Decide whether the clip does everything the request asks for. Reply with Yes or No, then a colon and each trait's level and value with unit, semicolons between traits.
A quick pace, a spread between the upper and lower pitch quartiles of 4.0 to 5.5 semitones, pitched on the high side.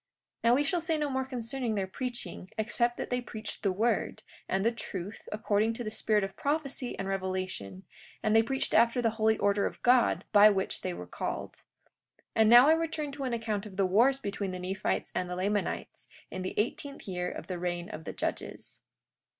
Yes: fast, 210 wpm; average, 4.4 semitones; high, 220 Hz